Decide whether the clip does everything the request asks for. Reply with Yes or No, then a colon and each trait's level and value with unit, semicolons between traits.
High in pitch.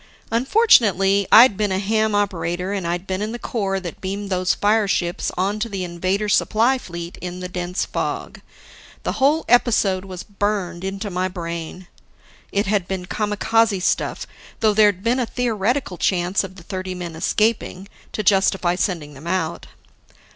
Yes: high, 195 Hz